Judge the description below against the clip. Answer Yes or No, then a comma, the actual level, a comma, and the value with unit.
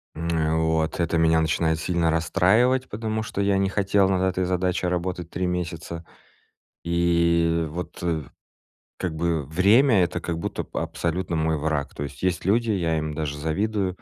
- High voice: No, very low, 85 Hz